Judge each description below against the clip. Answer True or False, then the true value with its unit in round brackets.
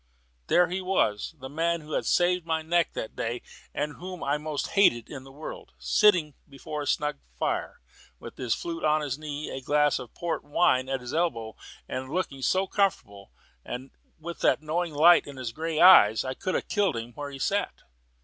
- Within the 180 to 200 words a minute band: True (195 wpm)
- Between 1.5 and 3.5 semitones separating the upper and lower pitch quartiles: False (4.6 semitones)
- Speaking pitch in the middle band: True (150 Hz)